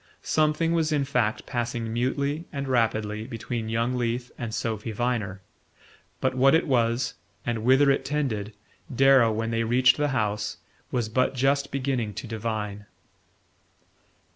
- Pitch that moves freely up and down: No, average, 3.4 semitones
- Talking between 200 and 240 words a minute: No, average, 140 wpm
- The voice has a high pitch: No, low, 120 Hz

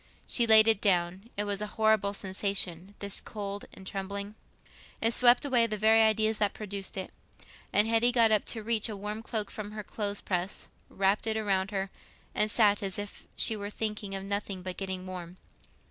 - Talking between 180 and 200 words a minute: Yes, average, 190 wpm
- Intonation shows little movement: Yes, narrow, 2.0 semitones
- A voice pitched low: No, high, 205 Hz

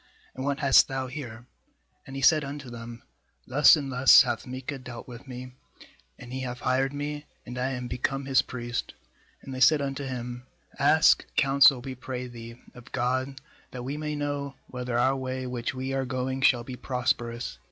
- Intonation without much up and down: Yes, narrow, 1.7 semitones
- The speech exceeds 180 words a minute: Yes, average, 190 wpm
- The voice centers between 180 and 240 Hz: No, low, 130 Hz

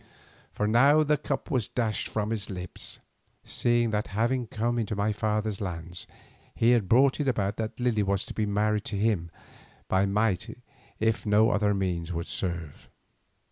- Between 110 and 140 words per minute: No, average, 170 wpm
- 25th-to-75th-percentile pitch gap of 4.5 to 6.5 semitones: No, average, 3.0 semitones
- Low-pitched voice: Yes, low, 105 Hz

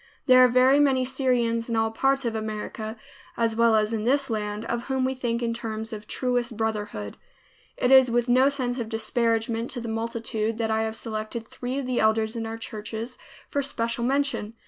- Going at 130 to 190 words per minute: No, average, 200 wpm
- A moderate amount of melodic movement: No, narrow, 2.3 semitones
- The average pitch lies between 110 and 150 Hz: No, high, 230 Hz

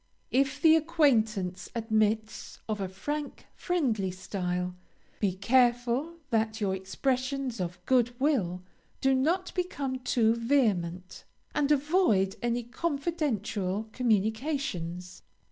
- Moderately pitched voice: No, high, 235 Hz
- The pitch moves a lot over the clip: Yes, wide, 6.1 semitones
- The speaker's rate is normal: No, slow, 105 wpm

